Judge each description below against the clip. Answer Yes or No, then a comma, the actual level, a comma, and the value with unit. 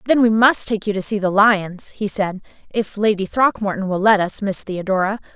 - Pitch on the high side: Yes, high, 205 Hz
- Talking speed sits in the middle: No, fast, 215 wpm